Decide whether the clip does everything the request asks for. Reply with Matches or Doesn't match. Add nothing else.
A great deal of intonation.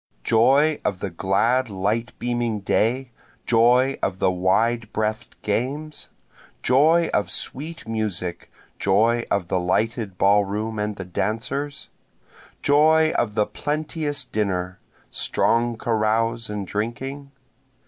Doesn't match